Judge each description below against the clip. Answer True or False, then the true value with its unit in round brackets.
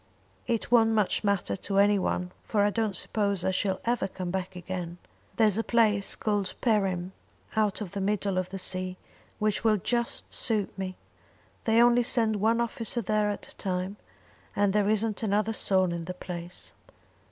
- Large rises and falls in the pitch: False (2.8 semitones)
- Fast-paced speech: False (175 wpm)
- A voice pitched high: True (205 Hz)